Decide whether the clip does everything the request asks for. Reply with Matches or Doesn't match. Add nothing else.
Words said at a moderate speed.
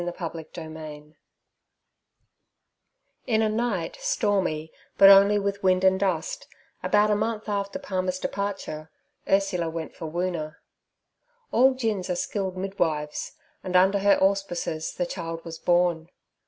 Doesn't match